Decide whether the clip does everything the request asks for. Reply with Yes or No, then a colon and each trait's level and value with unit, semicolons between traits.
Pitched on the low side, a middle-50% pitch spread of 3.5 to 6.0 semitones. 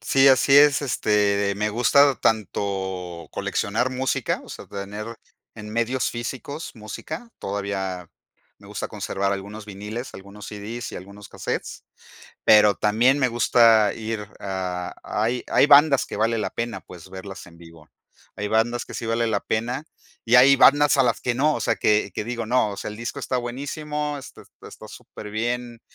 Yes: low, 110 Hz; average, 3.8 semitones